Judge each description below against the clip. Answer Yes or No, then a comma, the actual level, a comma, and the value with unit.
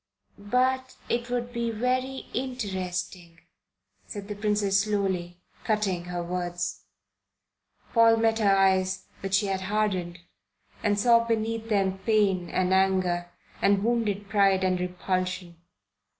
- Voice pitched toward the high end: Yes, high, 200 Hz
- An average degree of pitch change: Yes, average, 3.4 semitones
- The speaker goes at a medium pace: No, slow, 120 wpm